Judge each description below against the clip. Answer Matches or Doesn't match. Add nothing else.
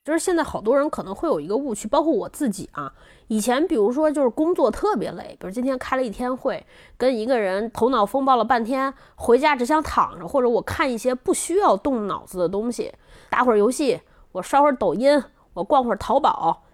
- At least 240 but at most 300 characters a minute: Doesn't match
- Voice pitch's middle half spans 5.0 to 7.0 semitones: Doesn't match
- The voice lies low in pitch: Doesn't match